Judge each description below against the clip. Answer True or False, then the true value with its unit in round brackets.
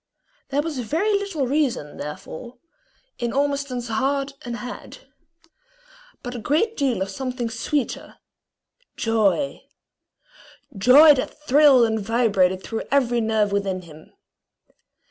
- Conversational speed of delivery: False (115 wpm)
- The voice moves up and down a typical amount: True (4.4 semitones)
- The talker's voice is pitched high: True (245 Hz)